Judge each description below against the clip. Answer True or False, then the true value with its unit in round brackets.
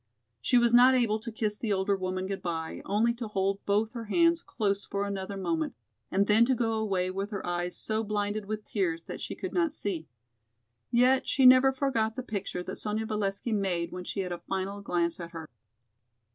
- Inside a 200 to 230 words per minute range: True (205 wpm)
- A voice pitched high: True (205 Hz)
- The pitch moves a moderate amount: True (3.3 semitones)